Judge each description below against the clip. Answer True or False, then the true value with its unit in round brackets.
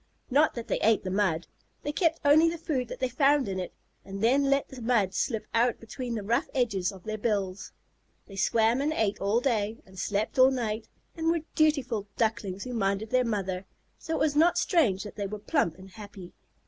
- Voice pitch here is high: True (225 Hz)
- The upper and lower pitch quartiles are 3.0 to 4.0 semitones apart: False (5.3 semitones)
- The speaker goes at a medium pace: False (210 wpm)